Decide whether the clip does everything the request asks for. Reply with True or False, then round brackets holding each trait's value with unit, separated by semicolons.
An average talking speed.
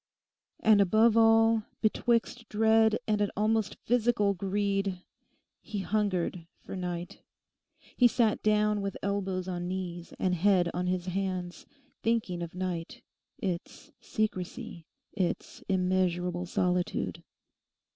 False (115 wpm)